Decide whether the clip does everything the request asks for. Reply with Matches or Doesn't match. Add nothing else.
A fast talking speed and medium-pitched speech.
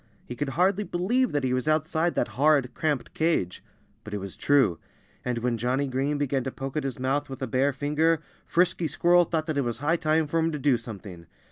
Matches